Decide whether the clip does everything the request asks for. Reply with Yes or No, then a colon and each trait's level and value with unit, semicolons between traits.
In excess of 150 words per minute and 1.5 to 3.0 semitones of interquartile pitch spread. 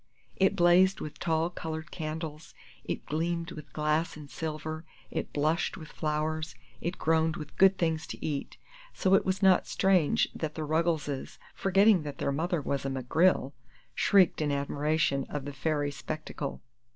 Yes: average, 160 wpm; narrow, 2.4 semitones